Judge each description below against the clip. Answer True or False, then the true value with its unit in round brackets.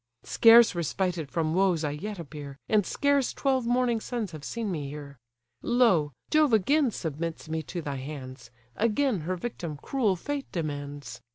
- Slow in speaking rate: False (160 wpm)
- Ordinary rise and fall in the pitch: False (7.8 semitones)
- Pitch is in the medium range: True (175 Hz)